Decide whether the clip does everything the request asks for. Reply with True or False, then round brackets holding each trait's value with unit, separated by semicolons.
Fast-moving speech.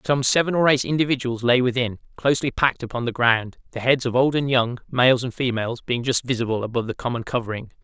True (215 wpm)